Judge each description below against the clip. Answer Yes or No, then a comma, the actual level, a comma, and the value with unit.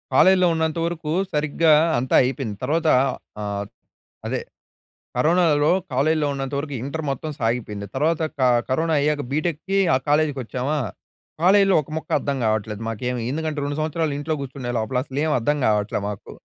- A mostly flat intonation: No, average, 4.2 semitones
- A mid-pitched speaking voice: Yes, medium, 145 Hz